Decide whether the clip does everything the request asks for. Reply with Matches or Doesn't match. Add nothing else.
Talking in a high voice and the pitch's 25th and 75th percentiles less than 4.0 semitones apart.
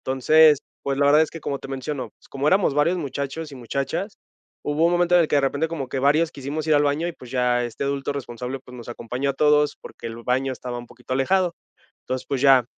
Doesn't match